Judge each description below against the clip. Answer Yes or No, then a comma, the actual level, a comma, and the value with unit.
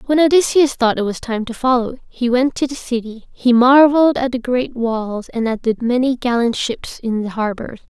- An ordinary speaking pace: No, fast, 210 wpm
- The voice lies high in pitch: Yes, high, 245 Hz